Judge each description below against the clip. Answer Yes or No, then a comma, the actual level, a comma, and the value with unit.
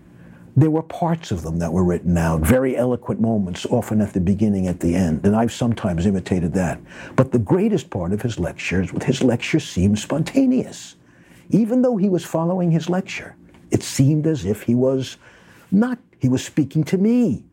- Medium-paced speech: Yes, average, 190 wpm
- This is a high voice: No, low, 120 Hz